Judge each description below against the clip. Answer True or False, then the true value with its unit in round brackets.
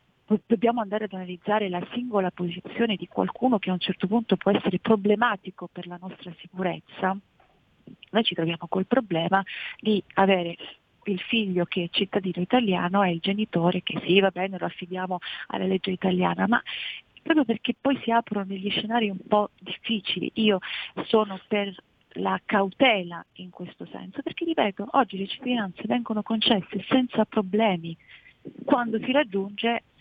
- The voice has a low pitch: False (200 Hz)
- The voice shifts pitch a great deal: False (3.6 semitones)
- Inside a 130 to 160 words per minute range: True (155 wpm)